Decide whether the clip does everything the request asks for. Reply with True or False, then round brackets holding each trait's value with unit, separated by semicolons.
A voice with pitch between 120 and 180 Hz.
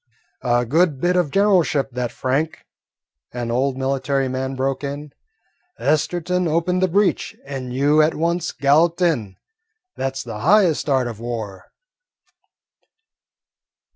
True (140 Hz)